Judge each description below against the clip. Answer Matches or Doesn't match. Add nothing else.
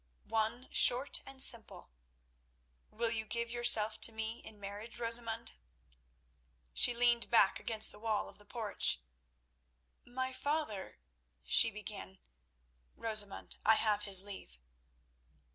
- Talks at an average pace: Doesn't match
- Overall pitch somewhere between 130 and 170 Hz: Doesn't match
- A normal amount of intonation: Doesn't match